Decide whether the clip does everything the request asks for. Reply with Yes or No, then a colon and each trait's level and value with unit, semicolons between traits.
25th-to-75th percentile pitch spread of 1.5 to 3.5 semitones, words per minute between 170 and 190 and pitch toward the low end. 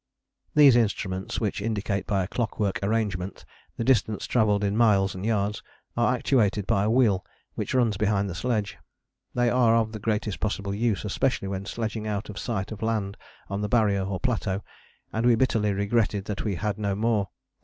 Yes: narrow, 2.5 semitones; average, 185 wpm; low, 105 Hz